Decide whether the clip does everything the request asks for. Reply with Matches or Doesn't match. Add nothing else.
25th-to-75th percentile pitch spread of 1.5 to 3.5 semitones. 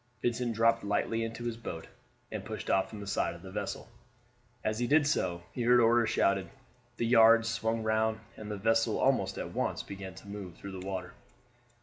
Matches